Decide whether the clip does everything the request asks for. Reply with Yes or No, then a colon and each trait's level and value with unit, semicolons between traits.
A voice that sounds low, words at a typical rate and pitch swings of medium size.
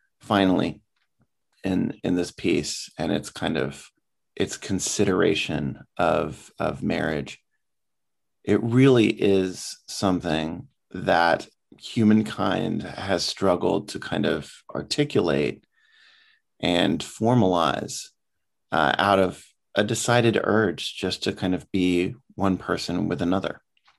No: low, 100 Hz; slow, 110 wpm; average, 3.7 semitones